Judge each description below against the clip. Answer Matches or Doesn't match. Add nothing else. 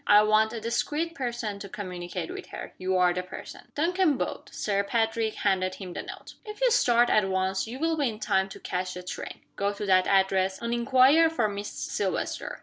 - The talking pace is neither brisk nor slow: Doesn't match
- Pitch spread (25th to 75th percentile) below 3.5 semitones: Doesn't match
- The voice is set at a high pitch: Matches